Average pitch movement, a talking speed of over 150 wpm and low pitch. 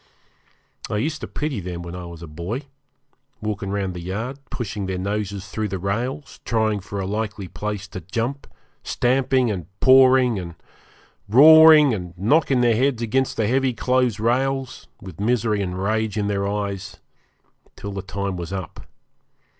Yes: average, 4.7 semitones; average, 160 wpm; low, 105 Hz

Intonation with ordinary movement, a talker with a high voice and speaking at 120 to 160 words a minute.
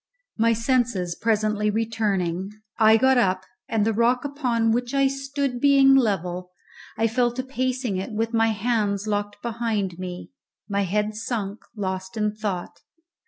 Yes: average, 3.3 semitones; high, 220 Hz; average, 150 wpm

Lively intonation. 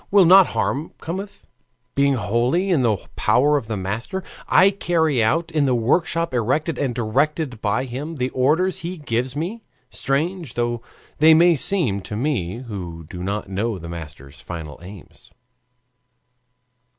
Yes: wide, 7.2 semitones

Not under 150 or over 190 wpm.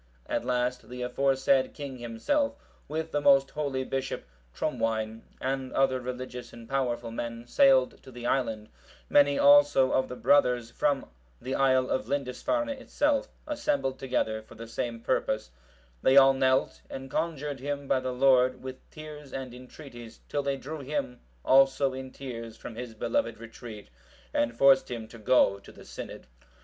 Yes: average, 160 wpm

